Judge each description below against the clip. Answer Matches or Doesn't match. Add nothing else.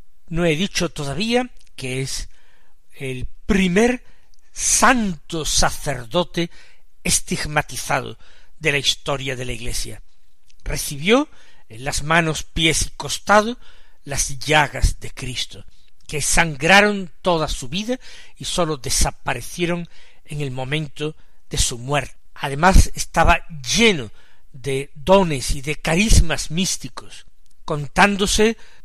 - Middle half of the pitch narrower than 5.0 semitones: Doesn't match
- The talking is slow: Matches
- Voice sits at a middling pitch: Matches